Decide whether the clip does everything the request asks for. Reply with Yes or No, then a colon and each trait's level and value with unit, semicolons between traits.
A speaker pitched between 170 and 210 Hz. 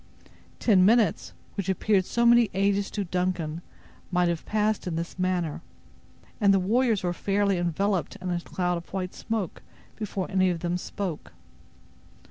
Yes: medium, 185 Hz